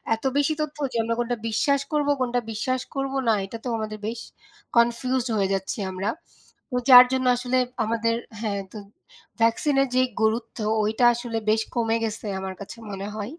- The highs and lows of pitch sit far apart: No, average, 2.9 semitones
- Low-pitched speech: No, high, 230 Hz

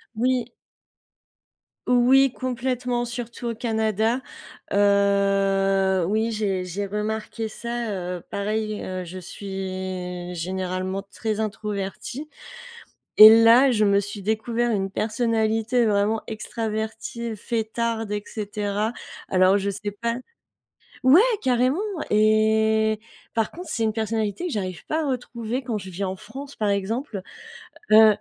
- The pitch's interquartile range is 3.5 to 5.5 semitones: No, average, 2.8 semitones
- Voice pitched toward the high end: Yes, high, 215 Hz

